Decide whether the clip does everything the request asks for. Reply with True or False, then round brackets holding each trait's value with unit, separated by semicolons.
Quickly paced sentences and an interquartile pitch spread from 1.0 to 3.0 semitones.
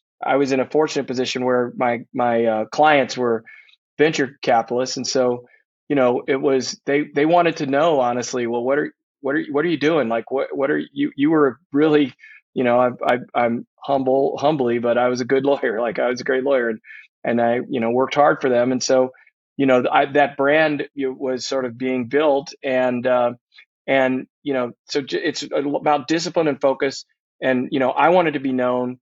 True (215 wpm; 2.6 semitones)